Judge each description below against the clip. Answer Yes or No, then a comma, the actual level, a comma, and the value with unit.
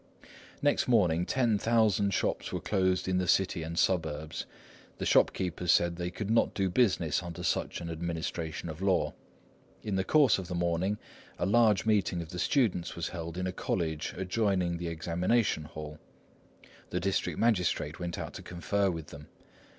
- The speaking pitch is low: Yes, very low, 90 Hz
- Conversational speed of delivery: Yes, average, 170 wpm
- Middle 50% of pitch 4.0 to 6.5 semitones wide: No, average, 2.9 semitones